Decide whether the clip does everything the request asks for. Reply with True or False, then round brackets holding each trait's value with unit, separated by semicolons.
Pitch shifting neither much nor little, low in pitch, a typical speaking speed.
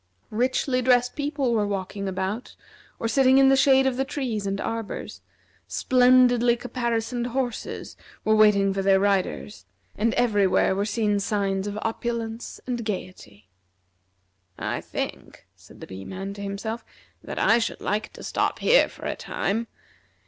False (3.8 semitones; 225 Hz; 150 wpm)